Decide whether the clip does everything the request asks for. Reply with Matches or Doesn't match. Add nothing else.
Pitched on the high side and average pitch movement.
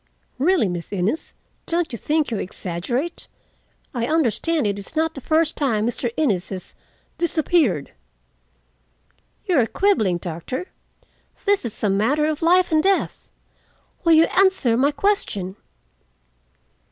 Doesn't match